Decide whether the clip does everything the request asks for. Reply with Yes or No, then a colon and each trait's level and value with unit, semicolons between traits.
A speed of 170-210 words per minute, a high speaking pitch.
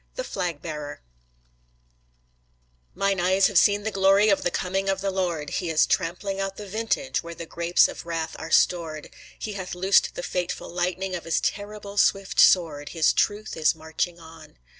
No: average, 180 wpm; medium, 180 Hz